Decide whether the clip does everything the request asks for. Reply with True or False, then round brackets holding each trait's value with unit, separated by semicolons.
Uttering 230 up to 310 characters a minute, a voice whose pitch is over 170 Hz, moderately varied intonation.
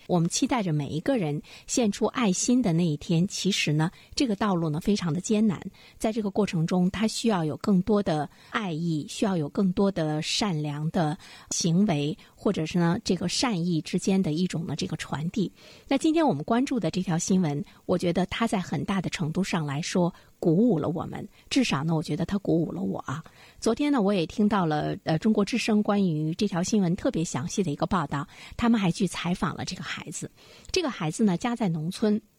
True (305 characters per minute; 185 Hz; 4.9 semitones)